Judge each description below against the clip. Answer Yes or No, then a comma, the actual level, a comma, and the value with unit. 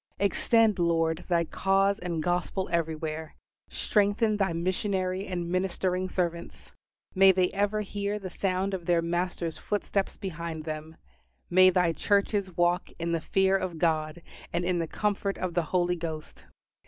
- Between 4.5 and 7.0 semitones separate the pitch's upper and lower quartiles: No, narrow, 2.5 semitones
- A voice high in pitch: No, medium, 180 Hz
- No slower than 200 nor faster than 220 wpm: No, average, 150 wpm